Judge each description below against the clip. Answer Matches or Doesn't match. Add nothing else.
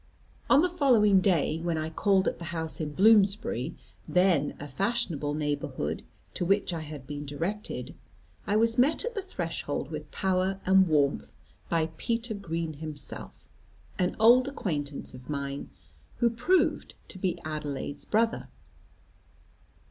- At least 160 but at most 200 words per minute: Doesn't match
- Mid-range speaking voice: Matches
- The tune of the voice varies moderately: Doesn't match